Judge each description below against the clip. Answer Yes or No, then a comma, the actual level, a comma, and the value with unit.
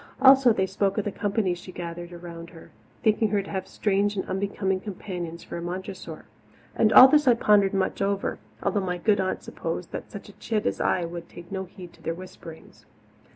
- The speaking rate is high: Yes, fast, 210 wpm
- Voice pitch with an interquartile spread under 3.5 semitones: Yes, average, 2.8 semitones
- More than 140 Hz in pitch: Yes, high, 190 Hz